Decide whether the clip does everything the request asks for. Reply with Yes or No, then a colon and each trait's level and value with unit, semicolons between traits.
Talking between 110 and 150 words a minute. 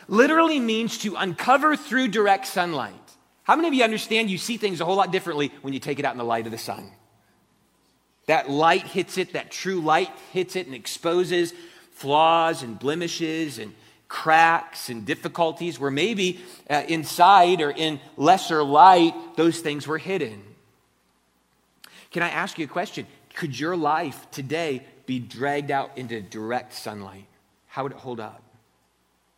No: average, 165 wpm